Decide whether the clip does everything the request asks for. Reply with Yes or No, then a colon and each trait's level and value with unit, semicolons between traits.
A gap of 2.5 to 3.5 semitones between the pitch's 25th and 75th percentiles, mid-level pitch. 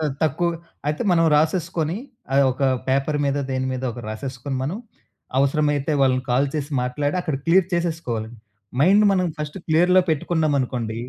No: average, 4.0 semitones; medium, 145 Hz